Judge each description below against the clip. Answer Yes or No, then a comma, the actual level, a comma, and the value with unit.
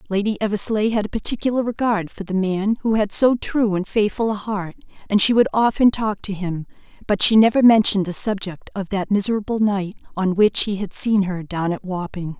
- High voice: Yes, high, 205 Hz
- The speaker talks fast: Yes, fast, 210 wpm